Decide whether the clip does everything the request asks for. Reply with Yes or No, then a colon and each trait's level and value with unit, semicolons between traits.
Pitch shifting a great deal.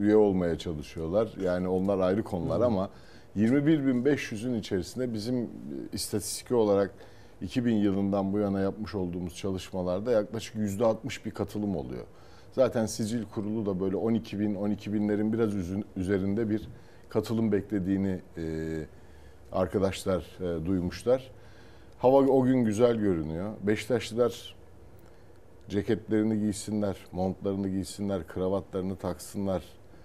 No: average, 3.2 semitones